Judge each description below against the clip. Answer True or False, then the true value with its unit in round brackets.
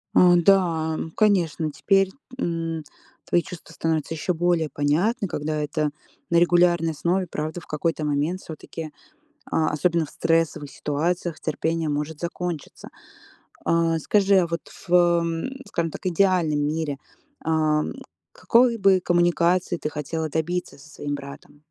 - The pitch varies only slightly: True (2.3 semitones)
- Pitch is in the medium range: True (165 Hz)